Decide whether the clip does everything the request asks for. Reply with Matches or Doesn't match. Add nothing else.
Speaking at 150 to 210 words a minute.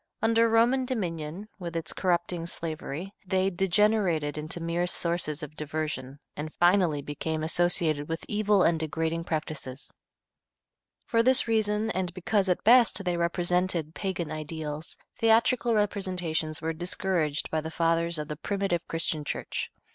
Doesn't match